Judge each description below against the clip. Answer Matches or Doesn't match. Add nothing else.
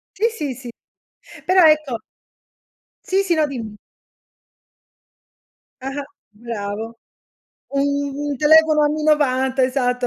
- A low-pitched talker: Doesn't match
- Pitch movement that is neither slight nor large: Matches